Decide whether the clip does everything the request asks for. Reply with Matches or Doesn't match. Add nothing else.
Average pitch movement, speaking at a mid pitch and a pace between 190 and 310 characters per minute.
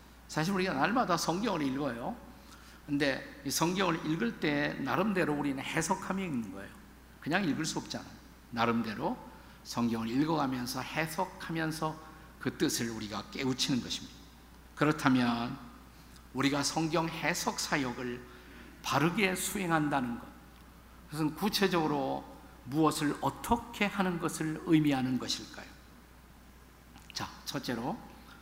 Matches